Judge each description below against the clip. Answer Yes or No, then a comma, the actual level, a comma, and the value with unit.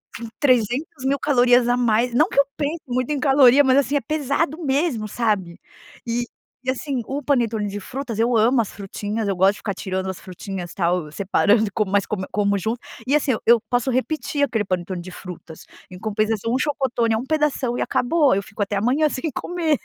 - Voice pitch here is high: Yes, high, 240 Hz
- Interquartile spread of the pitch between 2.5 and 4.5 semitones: No, average, 5.2 semitones